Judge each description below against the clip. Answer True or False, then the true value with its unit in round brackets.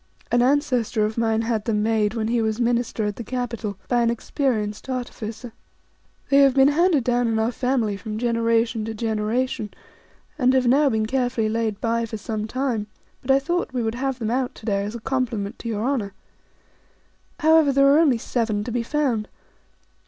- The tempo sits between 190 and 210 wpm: True (195 wpm)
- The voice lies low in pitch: False (235 Hz)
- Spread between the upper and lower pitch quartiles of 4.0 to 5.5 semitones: False (2.9 semitones)